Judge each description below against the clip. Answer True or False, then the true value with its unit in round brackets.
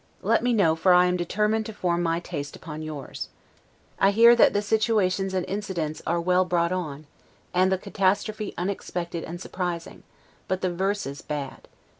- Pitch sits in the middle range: True (180 Hz)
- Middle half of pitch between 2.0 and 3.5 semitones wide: True (2.9 semitones)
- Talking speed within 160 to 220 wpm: True (170 wpm)